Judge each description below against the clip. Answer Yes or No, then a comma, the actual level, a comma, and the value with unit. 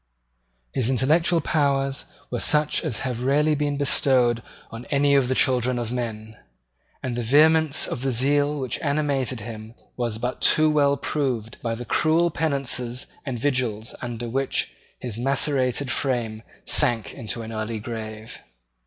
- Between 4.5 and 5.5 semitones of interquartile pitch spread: No, average, 3.5 semitones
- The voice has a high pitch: No, low, 130 Hz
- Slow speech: No, average, 150 wpm